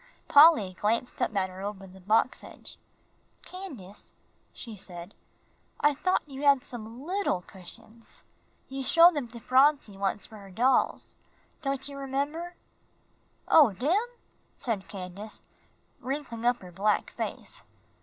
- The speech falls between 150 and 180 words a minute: No, slow, 135 wpm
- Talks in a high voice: Yes, high, 235 Hz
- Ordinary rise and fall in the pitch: No, wide, 6.1 semitones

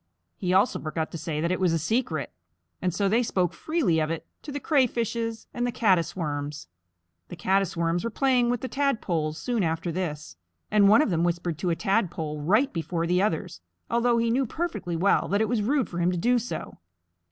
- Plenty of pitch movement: Yes, wide, 5.9 semitones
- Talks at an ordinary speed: No, fast, 210 wpm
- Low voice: No, medium, 185 Hz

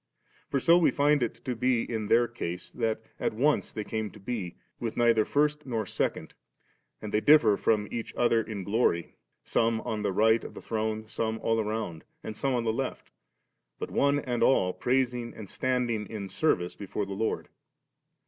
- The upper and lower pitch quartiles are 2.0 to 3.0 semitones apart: Yes, narrow, 2.6 semitones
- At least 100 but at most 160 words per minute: No, average, 185 wpm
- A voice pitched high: No, low, 115 Hz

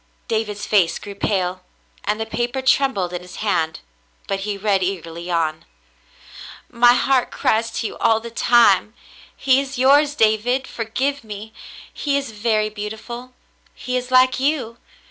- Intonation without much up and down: No, average, 4.0 semitones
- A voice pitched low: No, high, 220 Hz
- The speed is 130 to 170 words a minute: Yes, average, 160 wpm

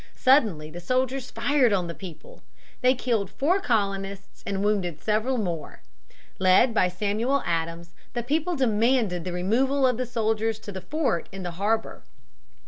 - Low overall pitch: No, high, 215 Hz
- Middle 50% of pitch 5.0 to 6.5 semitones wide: Yes, wide, 5.5 semitones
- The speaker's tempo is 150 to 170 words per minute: Yes, average, 155 wpm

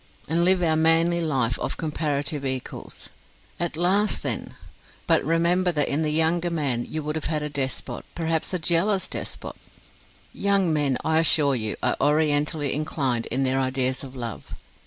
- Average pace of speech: Yes, average, 165 wpm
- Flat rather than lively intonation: No, average, 3.4 semitones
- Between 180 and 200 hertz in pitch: No, medium, 155 Hz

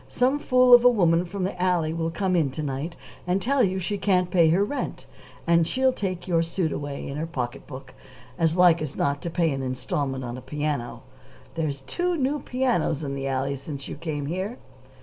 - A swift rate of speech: Yes, fast, 210 wpm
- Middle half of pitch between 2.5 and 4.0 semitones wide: No, average, 5.2 semitones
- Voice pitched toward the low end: No, medium, 165 Hz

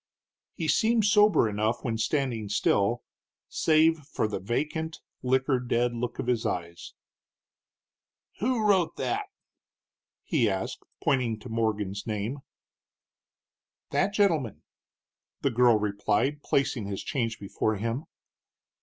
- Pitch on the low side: Yes, low, 120 Hz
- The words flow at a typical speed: No, slow, 115 wpm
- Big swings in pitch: Yes, wide, 6.3 semitones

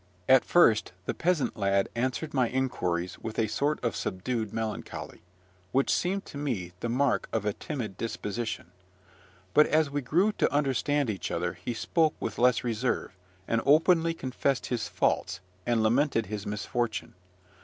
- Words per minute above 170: No, average, 155 wpm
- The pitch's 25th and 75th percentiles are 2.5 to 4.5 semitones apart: No, average, 4.9 semitones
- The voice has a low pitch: Yes, low, 120 Hz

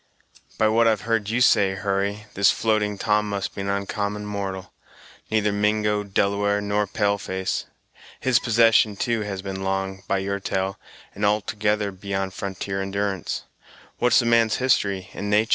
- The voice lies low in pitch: Yes, low, 100 Hz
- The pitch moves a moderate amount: No, narrow, 1.6 semitones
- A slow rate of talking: No, average, 160 wpm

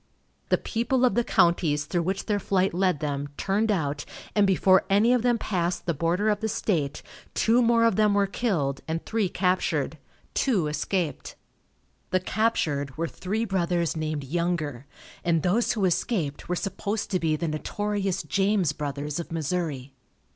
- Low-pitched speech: No, medium, 180 Hz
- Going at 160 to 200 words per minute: Yes, average, 165 wpm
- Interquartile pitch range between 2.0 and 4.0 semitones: No, average, 5.1 semitones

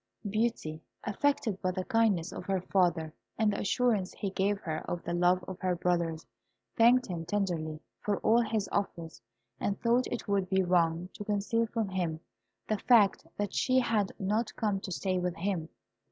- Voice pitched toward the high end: Yes, high, 195 Hz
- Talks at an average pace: Yes, average, 180 wpm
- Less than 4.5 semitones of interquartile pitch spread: Yes, average, 3.5 semitones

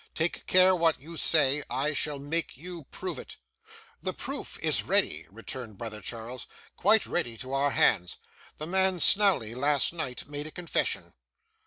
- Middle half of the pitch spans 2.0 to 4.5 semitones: No, average, 5.2 semitones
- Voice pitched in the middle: Yes, medium, 150 Hz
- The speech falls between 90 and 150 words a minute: No, average, 160 wpm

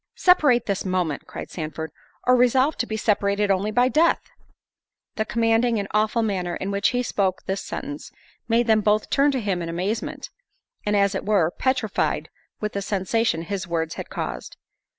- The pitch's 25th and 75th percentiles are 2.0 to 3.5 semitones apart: No, average, 3.9 semitones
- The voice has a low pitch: No, high, 210 Hz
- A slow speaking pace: No, average, 170 wpm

